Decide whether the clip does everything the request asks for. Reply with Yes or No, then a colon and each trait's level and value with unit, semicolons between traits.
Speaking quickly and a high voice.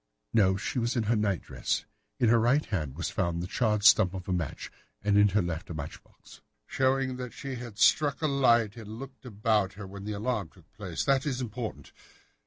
No: fast, 215 wpm; low, 110 Hz